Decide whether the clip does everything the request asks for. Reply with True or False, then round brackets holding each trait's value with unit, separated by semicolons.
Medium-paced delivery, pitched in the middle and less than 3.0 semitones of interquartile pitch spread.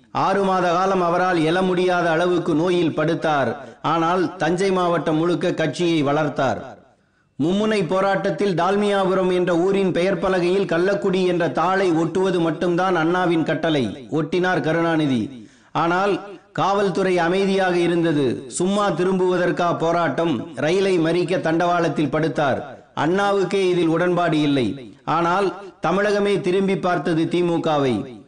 True (110 wpm; 175 Hz; 2.4 semitones)